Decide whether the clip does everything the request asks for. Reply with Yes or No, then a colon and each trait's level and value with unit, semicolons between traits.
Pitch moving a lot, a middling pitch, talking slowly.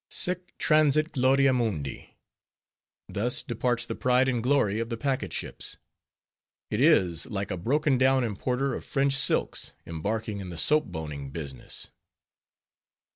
No: wide, 5.7 semitones; low, 125 Hz; slow, 130 wpm